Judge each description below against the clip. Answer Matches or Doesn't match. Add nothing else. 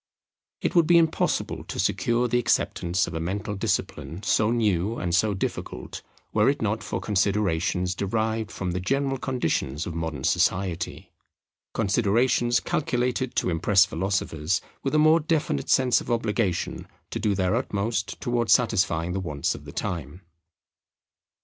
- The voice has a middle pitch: Doesn't match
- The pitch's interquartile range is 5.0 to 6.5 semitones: Matches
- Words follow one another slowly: Doesn't match